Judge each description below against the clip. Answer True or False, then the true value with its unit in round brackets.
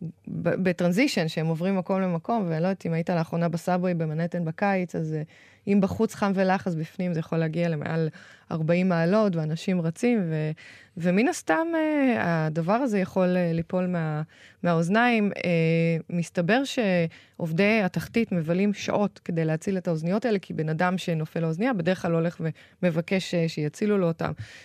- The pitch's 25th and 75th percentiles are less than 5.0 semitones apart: True (2.9 semitones)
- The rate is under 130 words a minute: False (150 wpm)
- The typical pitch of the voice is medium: True (175 Hz)